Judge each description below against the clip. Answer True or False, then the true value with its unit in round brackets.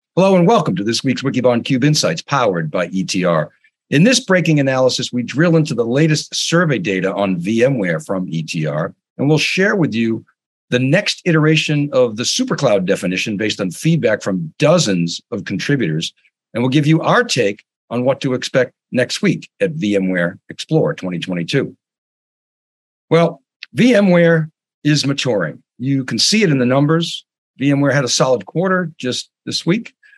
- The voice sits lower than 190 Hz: True (140 Hz)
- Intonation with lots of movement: True (6.1 semitones)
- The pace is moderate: True (160 wpm)